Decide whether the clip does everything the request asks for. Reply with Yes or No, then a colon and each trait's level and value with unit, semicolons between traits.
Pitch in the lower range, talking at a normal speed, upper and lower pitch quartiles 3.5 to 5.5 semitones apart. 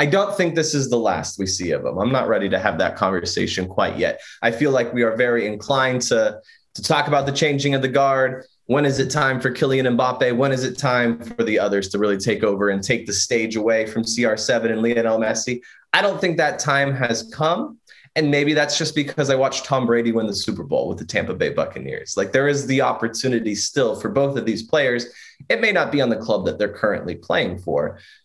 No: low, 130 Hz; fast, 240 wpm; average, 3.8 semitones